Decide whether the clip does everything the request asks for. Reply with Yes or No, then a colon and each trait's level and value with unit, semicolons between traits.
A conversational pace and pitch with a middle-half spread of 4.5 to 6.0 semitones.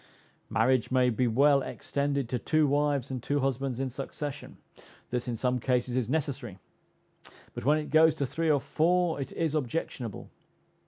No: average, 165 wpm; average, 2.8 semitones